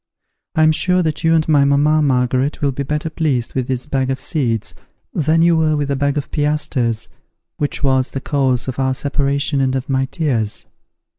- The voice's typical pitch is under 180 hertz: Yes, medium, 140 Hz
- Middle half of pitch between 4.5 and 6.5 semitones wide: No, average, 2.7 semitones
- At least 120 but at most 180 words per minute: No, average, 200 wpm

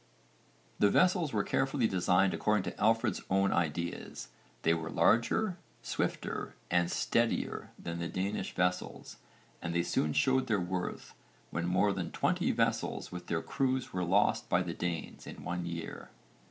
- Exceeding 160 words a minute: No, average, 155 wpm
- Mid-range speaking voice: No, very low, 90 Hz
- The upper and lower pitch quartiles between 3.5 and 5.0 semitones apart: Yes, average, 4.2 semitones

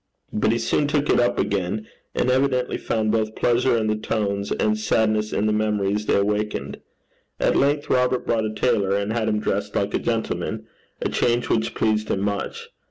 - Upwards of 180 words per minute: Yes, average, 190 wpm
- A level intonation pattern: Yes, narrow, 2.3 semitones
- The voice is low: Yes, low, 110 Hz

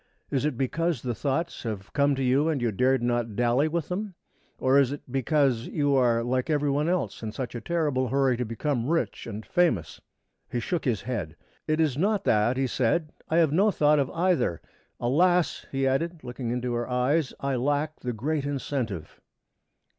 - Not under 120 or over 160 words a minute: No, average, 190 wpm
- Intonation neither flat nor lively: Yes, average, 4.3 semitones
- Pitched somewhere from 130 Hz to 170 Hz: Yes, low, 135 Hz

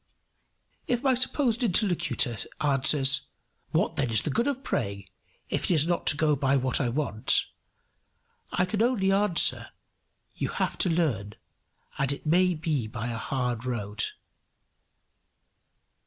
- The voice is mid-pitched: Yes, medium, 150 Hz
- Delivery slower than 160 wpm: Yes, average, 140 wpm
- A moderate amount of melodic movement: No, wide, 7.0 semitones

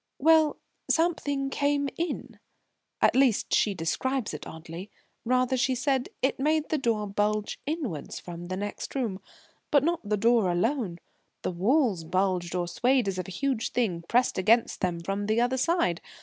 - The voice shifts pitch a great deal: Yes, wide, 6.5 semitones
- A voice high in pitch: Yes, high, 230 Hz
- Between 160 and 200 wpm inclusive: Yes, average, 165 wpm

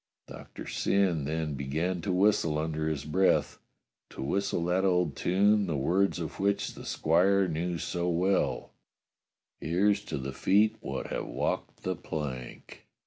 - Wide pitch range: No, average, 3.8 semitones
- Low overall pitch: Yes, very low, 90 Hz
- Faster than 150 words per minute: No, average, 145 wpm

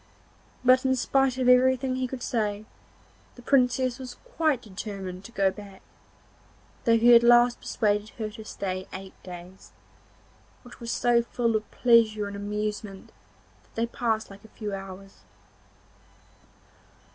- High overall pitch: Yes, high, 230 Hz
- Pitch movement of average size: Yes, average, 3.5 semitones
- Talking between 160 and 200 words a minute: No, average, 145 wpm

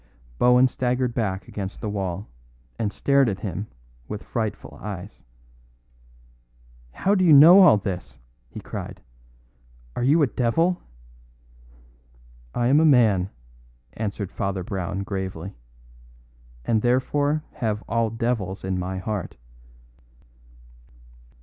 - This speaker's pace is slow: Yes, slow, 115 wpm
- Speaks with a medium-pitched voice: No, low, 110 Hz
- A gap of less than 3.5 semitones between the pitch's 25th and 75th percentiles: No, average, 4.8 semitones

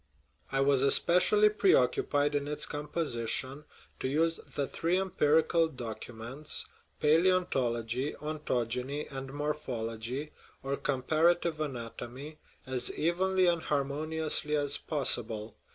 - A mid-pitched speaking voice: Yes, medium, 145 Hz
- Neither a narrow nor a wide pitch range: Yes, average, 3.8 semitones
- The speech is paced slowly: Yes, slow, 120 wpm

